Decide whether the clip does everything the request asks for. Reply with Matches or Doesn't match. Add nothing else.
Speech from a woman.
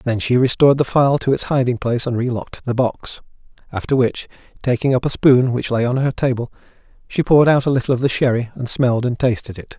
Doesn't match